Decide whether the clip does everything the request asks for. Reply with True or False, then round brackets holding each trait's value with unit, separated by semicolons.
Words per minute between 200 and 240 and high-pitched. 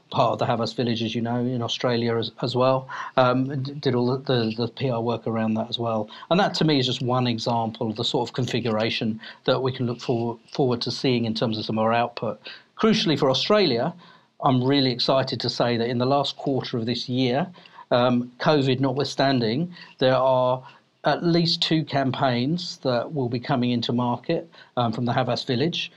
False (205 wpm; 125 Hz)